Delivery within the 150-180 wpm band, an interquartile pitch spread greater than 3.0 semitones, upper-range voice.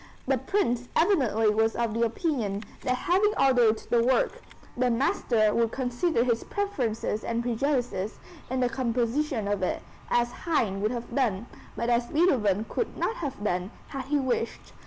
Yes: average, 160 wpm; average, 3.4 semitones; high, 240 Hz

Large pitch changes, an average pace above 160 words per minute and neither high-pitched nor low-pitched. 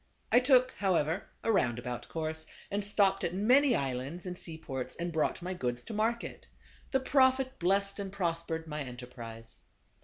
No: wide, 7.1 semitones; average, 155 wpm; medium, 175 Hz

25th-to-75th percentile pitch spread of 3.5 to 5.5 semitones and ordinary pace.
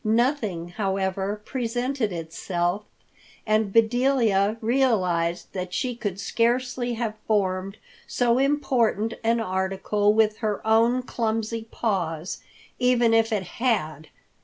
No: average, 3.8 semitones; slow, 110 wpm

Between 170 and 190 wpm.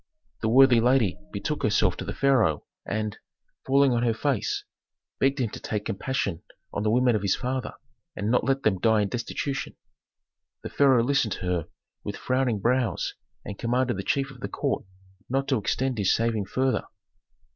Yes: average, 180 wpm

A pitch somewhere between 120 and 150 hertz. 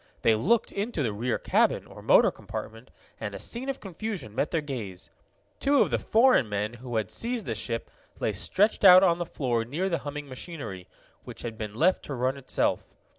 Yes: low, 135 Hz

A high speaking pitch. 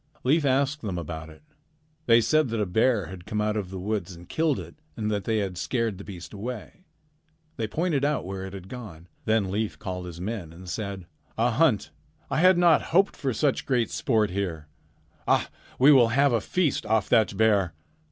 No: low, 110 Hz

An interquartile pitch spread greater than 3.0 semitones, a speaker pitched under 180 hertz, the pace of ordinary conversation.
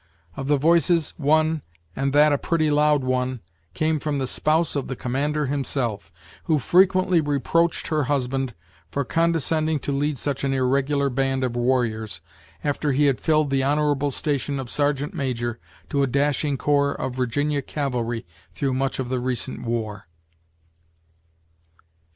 No: narrow, 2.6 semitones; medium, 140 Hz; average, 150 wpm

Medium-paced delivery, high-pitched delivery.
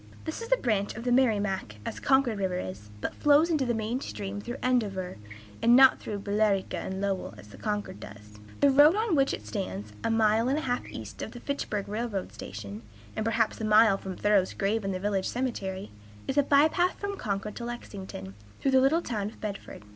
No: fast, 215 wpm; high, 215 Hz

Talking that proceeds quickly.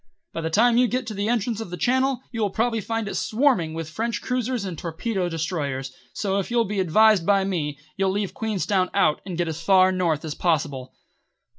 Yes: fast, 210 wpm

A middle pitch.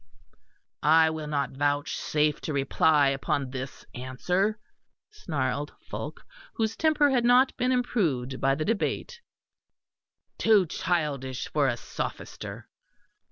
Yes: medium, 150 Hz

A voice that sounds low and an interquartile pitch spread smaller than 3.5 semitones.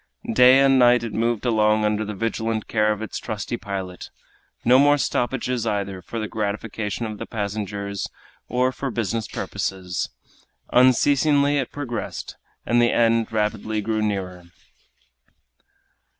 Yes: low, 110 Hz; average, 2.9 semitones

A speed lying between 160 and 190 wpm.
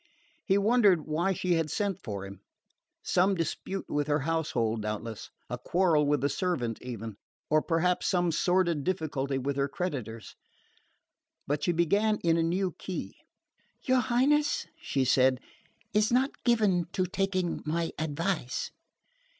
No: average, 140 wpm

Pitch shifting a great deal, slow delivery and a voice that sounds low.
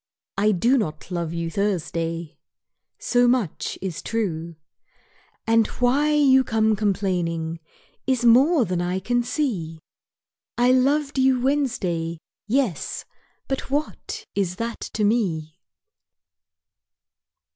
No: wide, 7.0 semitones; slow, 110 wpm; high, 215 Hz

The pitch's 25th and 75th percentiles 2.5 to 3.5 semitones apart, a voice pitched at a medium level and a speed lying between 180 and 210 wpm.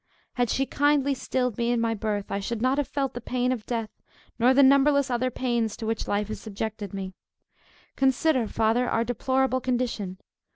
No: average, 3.0 semitones; high, 245 Hz; average, 190 wpm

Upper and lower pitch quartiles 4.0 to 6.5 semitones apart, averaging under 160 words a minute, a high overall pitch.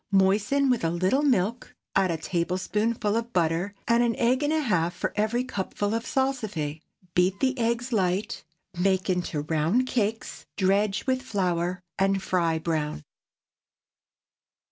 Yes: average, 4.7 semitones; average, 145 wpm; high, 200 Hz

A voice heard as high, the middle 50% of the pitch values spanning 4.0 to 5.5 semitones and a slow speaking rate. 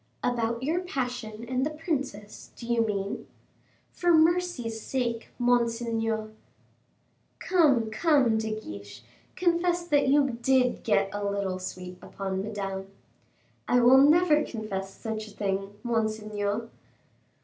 Yes: high, 230 Hz; average, 4.7 semitones; slow, 120 wpm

